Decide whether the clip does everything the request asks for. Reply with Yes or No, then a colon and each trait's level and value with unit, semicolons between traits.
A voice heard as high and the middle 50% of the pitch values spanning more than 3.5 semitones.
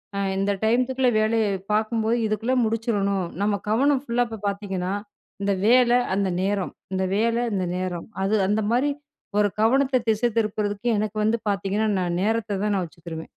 No: high, 215 Hz; average, 2.8 semitones